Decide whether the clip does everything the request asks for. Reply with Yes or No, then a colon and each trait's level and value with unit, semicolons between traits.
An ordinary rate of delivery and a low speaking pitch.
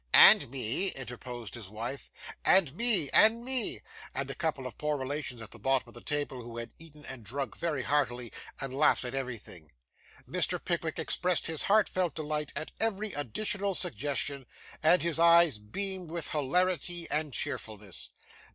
No: average, 160 wpm; medium, 145 Hz